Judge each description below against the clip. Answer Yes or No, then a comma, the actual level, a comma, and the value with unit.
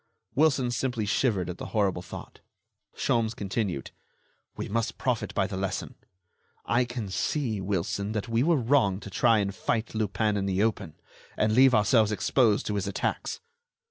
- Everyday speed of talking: Yes, average, 165 wpm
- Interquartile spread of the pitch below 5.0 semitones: Yes, average, 3.2 semitones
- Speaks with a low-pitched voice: Yes, low, 110 Hz